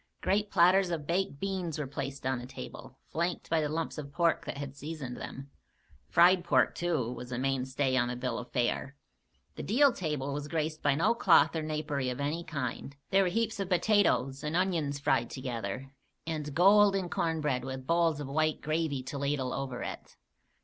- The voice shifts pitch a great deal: No, average, 4.1 semitones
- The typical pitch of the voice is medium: Yes, medium, 150 Hz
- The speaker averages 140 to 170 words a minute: No, average, 190 wpm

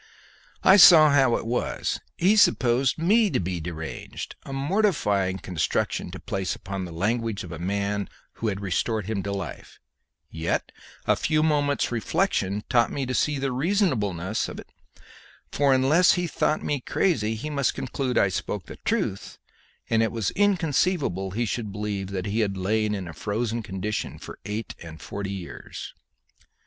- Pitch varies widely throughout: Yes, wide, 6.5 semitones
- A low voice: Yes, low, 110 Hz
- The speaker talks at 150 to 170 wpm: Yes, average, 160 wpm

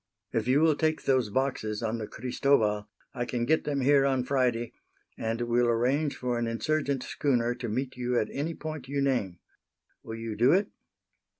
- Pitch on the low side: Yes, low, 125 Hz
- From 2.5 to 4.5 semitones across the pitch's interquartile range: Yes, average, 3.2 semitones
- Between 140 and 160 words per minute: No, average, 185 wpm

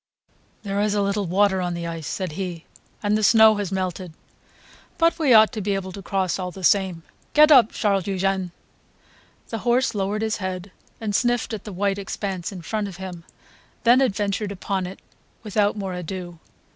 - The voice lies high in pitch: Yes, high, 195 Hz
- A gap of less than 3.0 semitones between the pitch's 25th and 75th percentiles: Yes, narrow, 2.4 semitones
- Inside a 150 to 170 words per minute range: No, average, 185 wpm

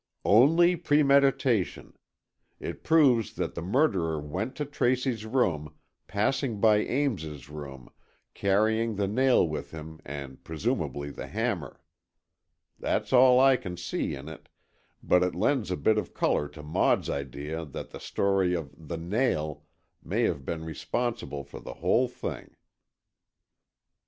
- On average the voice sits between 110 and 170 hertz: No, low, 100 Hz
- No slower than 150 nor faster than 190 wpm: No, slow, 135 wpm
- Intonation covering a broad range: Yes, wide, 8.5 semitones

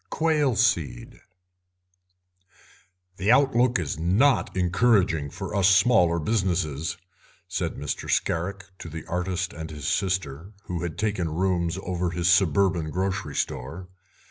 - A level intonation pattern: No, average, 3.2 semitones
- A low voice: Yes, very low, 90 Hz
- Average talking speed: No, slow, 120 wpm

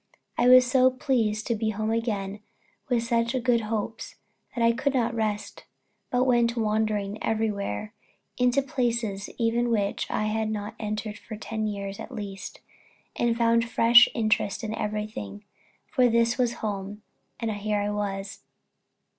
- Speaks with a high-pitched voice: Yes, high, 220 Hz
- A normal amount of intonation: No, narrow, 2.2 semitones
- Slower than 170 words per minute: Yes, average, 155 wpm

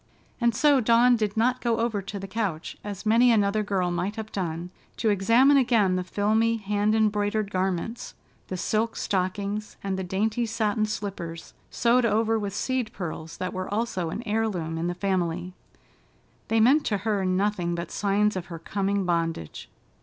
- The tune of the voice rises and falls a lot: No, average, 3.4 semitones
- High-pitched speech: Yes, high, 205 Hz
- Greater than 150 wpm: Yes, average, 170 wpm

